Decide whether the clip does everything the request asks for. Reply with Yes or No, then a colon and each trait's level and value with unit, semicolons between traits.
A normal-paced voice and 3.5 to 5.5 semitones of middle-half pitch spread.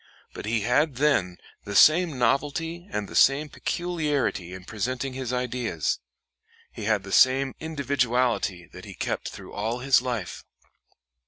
Yes: average, 145 wpm; average, 4.9 semitones